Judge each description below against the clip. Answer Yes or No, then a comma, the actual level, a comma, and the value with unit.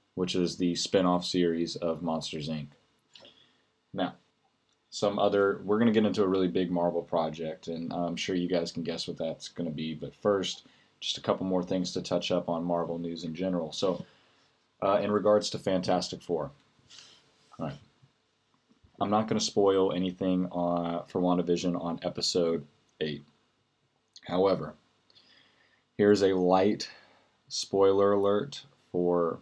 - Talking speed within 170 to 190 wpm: No, average, 155 wpm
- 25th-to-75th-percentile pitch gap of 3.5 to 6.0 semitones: No, narrow, 2.6 semitones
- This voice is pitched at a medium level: No, very low, 90 Hz